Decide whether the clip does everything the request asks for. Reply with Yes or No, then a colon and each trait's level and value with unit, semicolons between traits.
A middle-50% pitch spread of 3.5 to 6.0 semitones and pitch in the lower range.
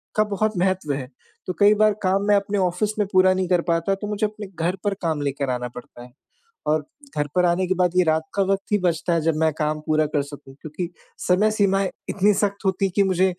No: average, 4.1 semitones; medium, 185 Hz